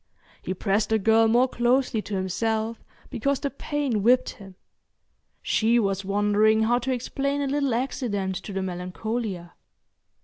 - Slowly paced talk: No, average, 145 wpm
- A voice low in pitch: No, high, 220 Hz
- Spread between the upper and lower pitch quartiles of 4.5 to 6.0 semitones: No, average, 4.0 semitones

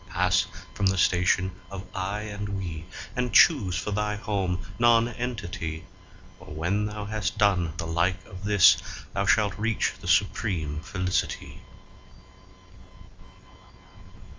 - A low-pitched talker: Yes, very low, 95 Hz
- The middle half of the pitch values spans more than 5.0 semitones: No, average, 2.7 semitones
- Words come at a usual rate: No, slow, 115 wpm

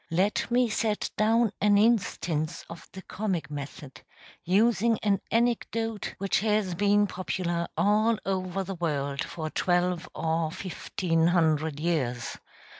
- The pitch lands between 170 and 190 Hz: Yes, medium, 185 Hz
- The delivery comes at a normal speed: No, slow, 125 wpm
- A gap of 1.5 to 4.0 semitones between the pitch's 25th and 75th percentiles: No, average, 4.4 semitones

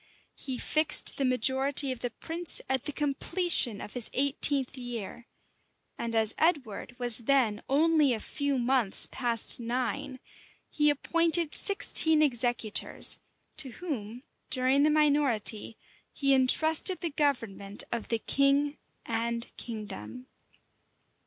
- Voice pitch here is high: Yes, very high, 260 Hz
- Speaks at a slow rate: Yes, slow, 120 wpm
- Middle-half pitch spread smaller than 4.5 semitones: Yes, average, 3.9 semitones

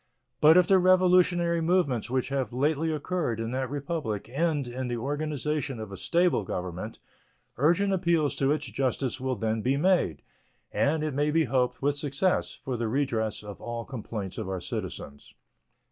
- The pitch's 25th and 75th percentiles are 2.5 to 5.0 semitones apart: No, wide, 5.4 semitones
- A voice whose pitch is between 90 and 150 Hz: Yes, medium, 140 Hz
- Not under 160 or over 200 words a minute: Yes, average, 170 wpm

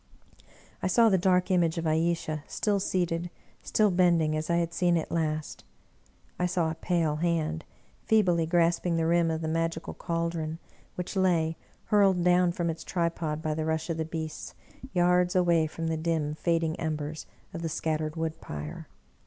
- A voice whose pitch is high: No, medium, 165 Hz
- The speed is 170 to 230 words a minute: Yes, average, 180 wpm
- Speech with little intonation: Yes, narrow, 1.8 semitones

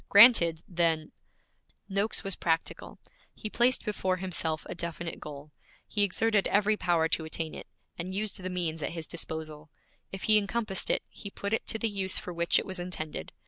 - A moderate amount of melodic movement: Yes, average, 3.9 semitones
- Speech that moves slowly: No, average, 185 wpm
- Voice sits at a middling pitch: Yes, medium, 180 Hz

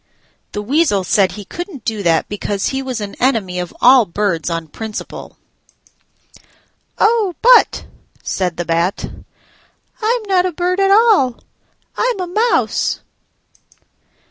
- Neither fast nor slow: No, slow, 130 wpm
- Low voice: No, high, 245 Hz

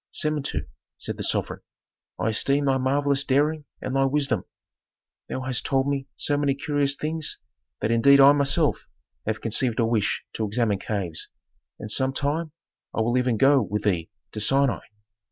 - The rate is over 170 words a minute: No, average, 165 wpm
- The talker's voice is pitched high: No, low, 135 Hz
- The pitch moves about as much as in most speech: Yes, average, 4.1 semitones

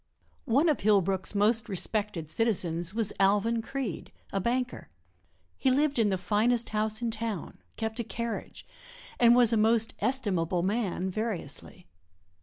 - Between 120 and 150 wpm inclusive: Yes, average, 140 wpm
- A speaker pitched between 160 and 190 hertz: No, high, 220 Hz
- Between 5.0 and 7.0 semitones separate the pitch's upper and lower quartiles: No, average, 3.3 semitones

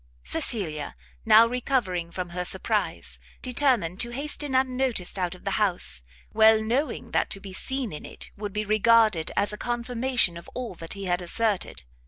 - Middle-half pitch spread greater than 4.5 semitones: Yes, average, 5.3 semitones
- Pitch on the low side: No, high, 215 Hz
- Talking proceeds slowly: No, average, 170 wpm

